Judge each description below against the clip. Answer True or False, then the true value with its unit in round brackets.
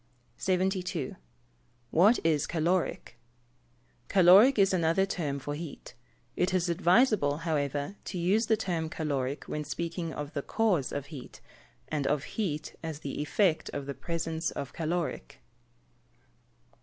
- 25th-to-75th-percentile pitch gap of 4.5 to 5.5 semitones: False (4.0 semitones)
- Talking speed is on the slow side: True (130 wpm)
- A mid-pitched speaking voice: True (165 Hz)